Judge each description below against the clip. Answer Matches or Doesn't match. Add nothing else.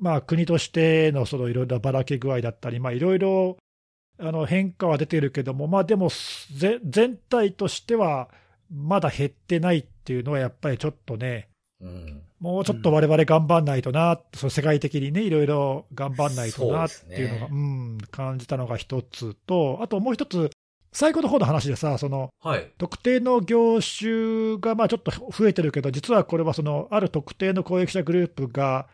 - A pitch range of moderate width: Doesn't match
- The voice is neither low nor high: Matches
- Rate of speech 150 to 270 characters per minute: Doesn't match